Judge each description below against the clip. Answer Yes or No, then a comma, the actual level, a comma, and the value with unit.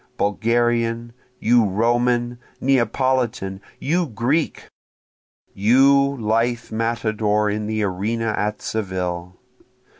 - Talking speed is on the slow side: Yes, slow, 85 wpm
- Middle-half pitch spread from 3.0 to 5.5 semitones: No, narrow, 2.4 semitones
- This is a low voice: Yes, low, 115 Hz